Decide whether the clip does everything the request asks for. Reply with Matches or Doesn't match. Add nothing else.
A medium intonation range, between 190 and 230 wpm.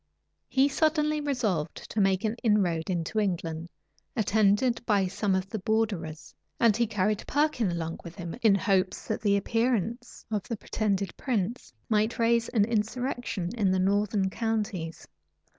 Doesn't match